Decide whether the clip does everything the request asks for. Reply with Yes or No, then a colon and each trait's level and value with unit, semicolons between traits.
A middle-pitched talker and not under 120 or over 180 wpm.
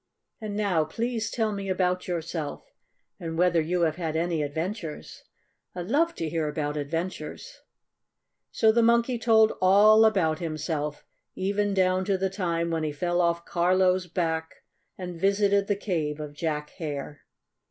Yes: medium, 180 Hz; average, 150 wpm